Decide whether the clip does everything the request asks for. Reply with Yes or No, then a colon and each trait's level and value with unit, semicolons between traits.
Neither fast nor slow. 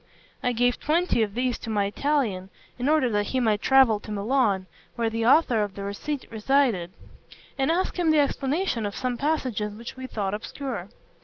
Yes: average, 185 wpm